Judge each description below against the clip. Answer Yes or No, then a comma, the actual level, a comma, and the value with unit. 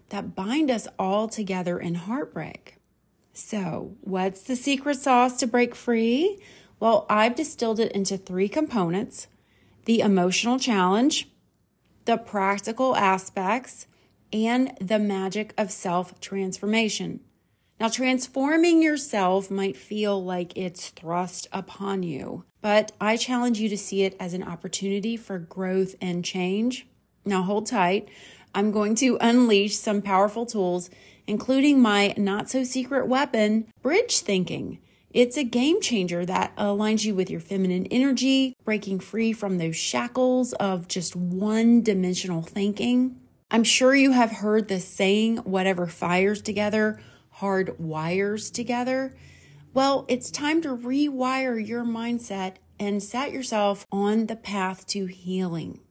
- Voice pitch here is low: No, high, 210 Hz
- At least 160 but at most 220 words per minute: No, slow, 135 wpm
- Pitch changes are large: No, average, 4.3 semitones